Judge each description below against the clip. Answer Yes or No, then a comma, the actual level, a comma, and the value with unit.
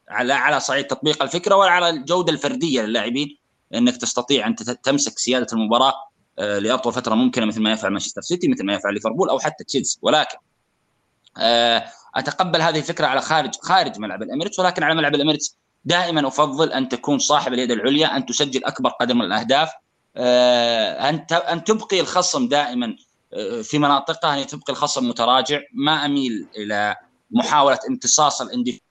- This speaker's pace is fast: Yes, fast, 150 wpm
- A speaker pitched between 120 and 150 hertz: Yes, medium, 140 Hz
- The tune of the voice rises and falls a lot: No, average, 4.5 semitones